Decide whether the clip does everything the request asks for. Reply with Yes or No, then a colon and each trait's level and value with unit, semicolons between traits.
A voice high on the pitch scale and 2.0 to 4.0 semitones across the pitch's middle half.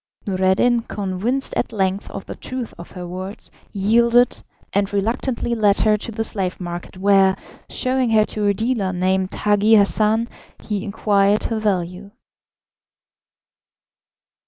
Yes: high, 205 Hz; average, 2.8 semitones